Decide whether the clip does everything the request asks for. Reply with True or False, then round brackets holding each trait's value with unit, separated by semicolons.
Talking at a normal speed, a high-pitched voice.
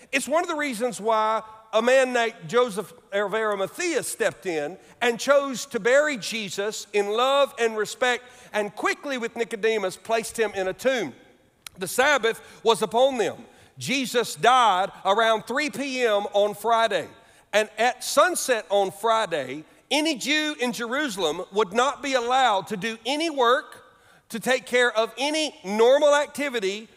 True (150 wpm; 235 Hz)